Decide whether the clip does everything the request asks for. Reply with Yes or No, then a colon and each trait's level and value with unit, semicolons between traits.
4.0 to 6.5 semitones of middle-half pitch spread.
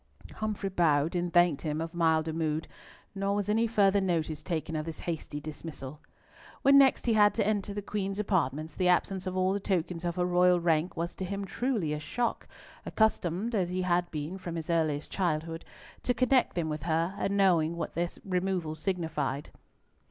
No: average, 3.5 semitones